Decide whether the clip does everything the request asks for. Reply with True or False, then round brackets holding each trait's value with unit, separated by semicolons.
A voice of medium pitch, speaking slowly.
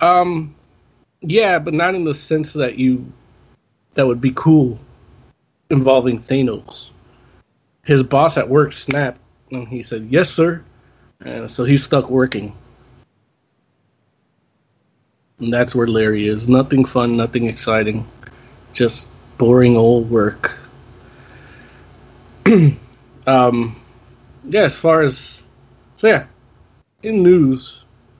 False (125 Hz; 110 wpm)